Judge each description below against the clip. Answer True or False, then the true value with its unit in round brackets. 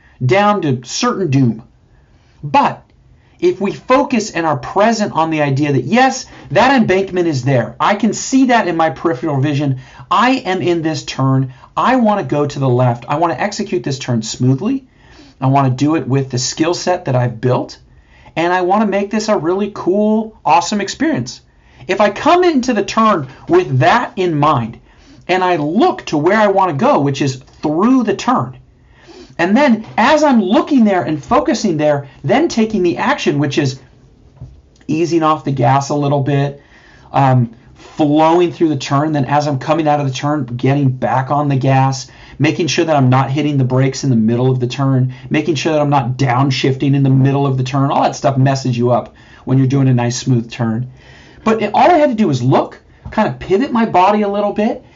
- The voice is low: False (150 Hz)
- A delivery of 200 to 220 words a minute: True (205 wpm)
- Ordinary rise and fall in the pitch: False (7.1 semitones)